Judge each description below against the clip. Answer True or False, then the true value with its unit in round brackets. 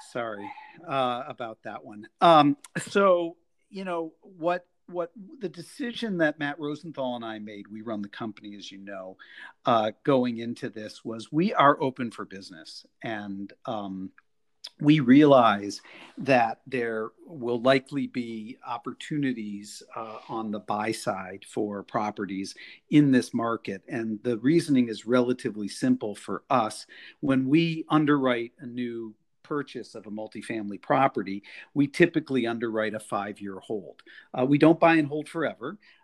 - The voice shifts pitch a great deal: True (5.8 semitones)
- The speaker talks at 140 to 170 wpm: True (145 wpm)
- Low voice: True (125 Hz)